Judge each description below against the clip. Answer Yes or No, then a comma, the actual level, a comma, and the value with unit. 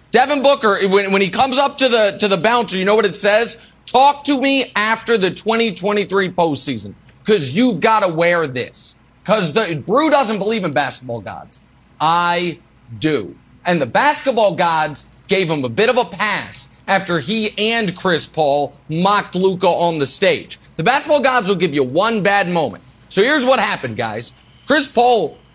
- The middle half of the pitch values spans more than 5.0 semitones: Yes, wide, 5.4 semitones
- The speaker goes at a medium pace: Yes, average, 180 wpm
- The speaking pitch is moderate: No, high, 200 Hz